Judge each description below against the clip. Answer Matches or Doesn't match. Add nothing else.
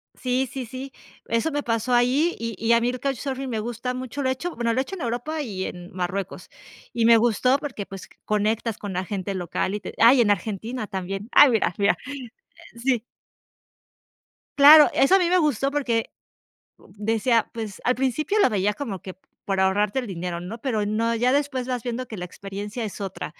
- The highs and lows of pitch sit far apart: Doesn't match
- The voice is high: Matches